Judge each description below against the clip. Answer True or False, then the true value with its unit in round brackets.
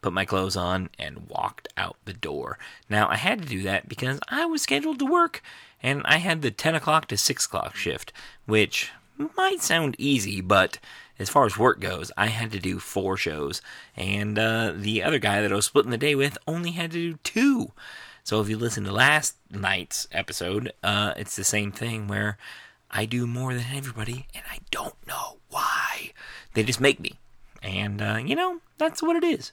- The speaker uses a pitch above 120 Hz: False (115 Hz)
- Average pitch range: False (7.3 semitones)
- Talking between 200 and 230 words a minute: True (205 wpm)